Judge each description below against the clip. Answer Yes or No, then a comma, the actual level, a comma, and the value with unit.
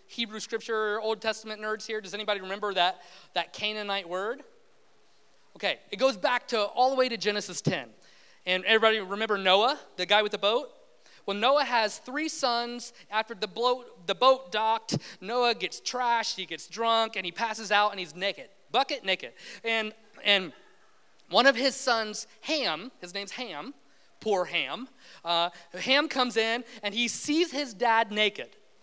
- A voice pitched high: Yes, high, 220 Hz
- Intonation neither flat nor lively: Yes, average, 3.6 semitones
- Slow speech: No, average, 165 wpm